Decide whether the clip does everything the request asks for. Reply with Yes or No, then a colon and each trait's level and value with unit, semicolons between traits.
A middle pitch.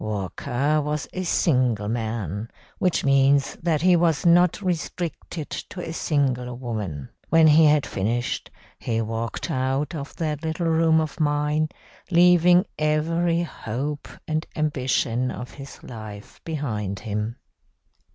Yes: medium, 145 Hz